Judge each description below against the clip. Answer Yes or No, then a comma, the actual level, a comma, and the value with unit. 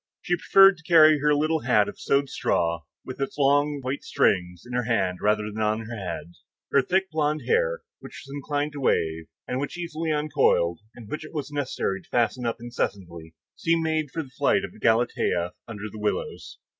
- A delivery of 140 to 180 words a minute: No, average, 195 wpm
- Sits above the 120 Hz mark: Yes, low, 135 Hz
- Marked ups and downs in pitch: Yes, wide, 6.4 semitones